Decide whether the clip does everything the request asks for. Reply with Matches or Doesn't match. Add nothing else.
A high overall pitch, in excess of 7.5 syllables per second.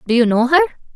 Matches